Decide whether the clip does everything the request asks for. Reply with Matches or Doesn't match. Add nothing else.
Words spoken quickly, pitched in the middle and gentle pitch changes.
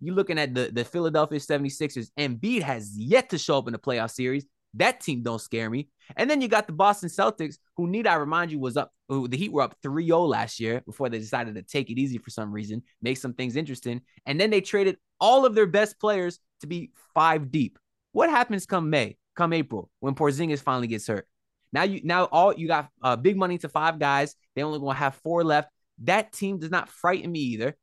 Doesn't match